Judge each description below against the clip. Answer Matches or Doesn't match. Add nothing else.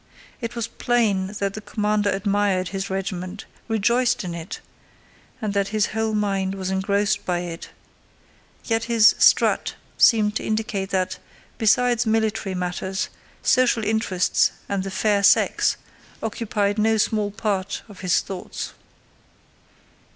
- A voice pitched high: Matches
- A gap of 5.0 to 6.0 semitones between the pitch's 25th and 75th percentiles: Doesn't match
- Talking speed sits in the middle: Doesn't match